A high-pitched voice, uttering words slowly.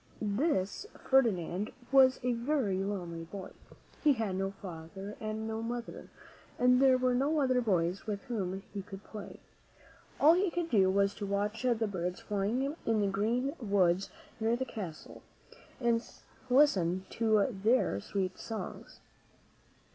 No: high, 215 Hz; average, 145 wpm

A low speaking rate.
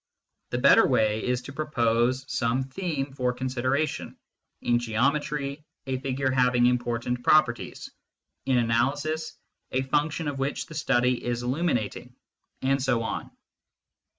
Yes: slow, 125 wpm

